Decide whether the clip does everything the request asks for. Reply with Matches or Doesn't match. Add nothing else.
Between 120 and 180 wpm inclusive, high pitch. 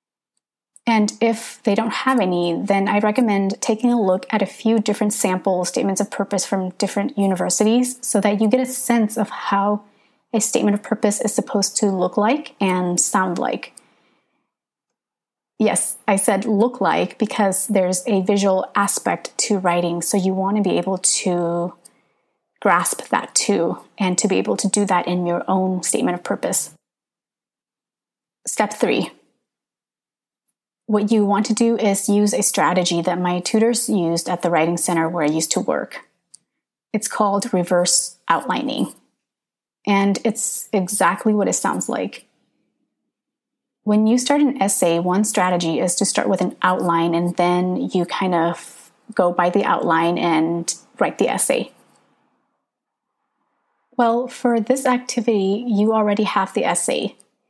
Matches